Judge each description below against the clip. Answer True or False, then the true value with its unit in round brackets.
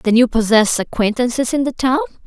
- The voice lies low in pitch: False (245 Hz)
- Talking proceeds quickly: False (185 wpm)